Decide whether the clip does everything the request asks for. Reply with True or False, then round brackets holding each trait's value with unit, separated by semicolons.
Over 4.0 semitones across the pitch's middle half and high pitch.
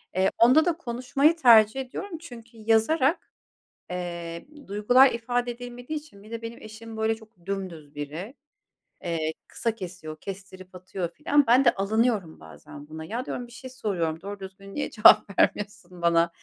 True (5.1 semitones; 215 Hz)